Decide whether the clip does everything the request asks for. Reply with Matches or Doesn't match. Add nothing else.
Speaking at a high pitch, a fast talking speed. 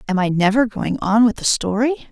Matches